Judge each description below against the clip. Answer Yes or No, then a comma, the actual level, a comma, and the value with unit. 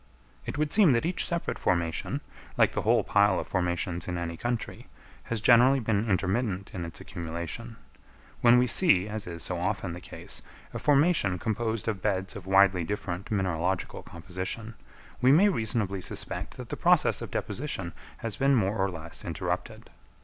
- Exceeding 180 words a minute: No, average, 170 wpm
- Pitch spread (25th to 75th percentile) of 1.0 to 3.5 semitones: No, average, 4.7 semitones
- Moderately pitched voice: No, low, 100 Hz